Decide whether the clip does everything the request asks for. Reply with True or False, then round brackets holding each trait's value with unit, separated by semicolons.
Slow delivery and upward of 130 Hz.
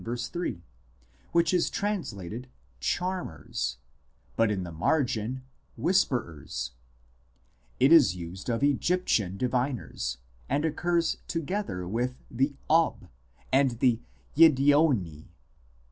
False (105 wpm; 125 Hz)